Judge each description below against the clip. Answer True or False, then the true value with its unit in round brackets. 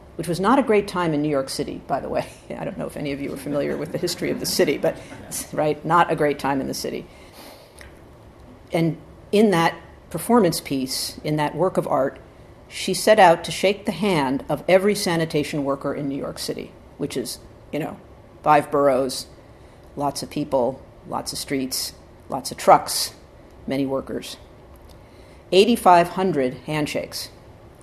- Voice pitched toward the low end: False (150 Hz)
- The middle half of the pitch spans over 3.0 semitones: True (4.5 semitones)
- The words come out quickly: False (175 wpm)